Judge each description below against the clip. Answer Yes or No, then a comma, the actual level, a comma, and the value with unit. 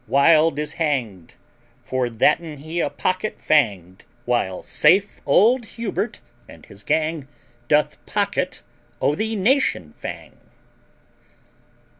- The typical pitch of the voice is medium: Yes, medium, 150 Hz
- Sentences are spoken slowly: Yes, slow, 110 wpm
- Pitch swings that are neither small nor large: No, wide, 7.0 semitones